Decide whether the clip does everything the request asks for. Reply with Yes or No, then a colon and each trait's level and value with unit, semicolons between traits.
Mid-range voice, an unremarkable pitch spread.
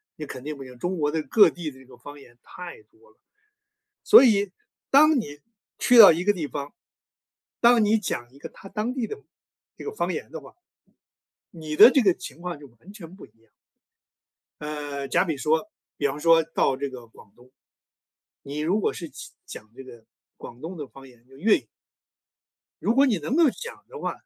No: medium, 160 Hz; wide, 7.3 semitones